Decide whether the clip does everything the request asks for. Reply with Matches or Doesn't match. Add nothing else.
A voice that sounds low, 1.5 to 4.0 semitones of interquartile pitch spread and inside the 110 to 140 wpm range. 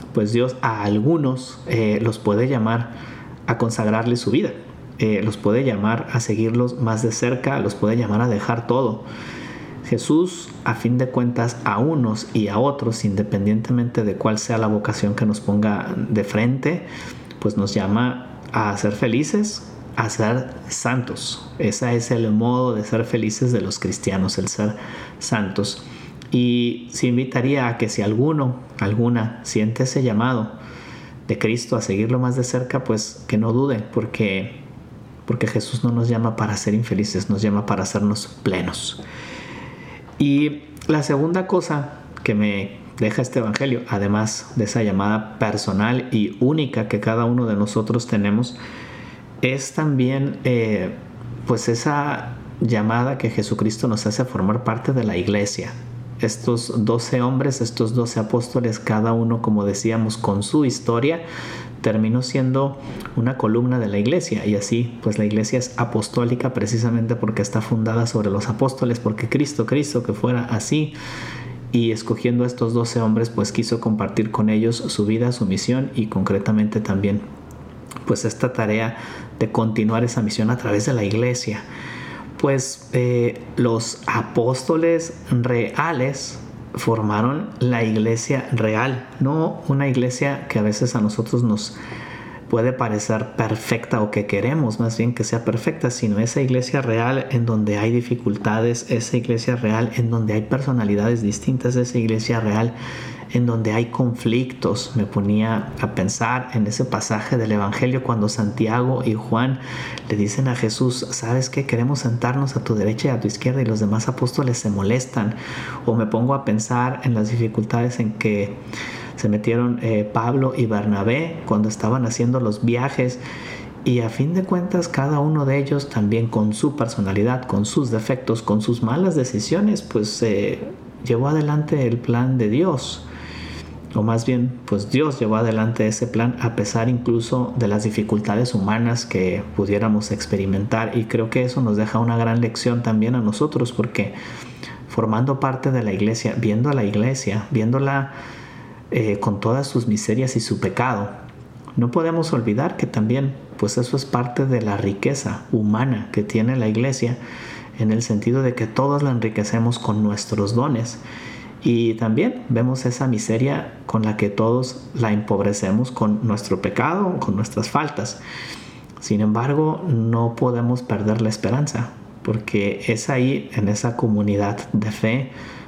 Doesn't match